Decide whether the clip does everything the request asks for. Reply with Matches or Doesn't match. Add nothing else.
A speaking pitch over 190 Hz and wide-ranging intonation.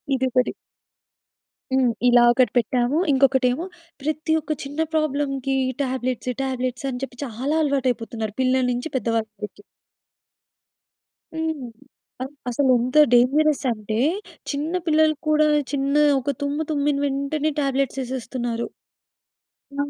Doesn't match